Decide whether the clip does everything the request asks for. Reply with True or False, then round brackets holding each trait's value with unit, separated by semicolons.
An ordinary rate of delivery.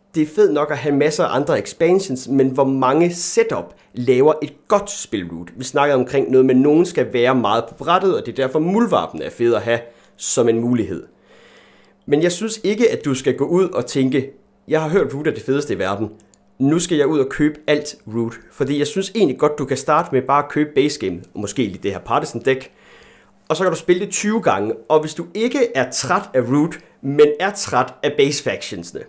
False (235 wpm)